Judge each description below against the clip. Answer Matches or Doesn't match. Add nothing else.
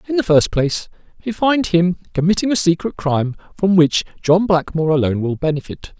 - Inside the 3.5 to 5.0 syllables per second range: Doesn't match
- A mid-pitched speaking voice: Matches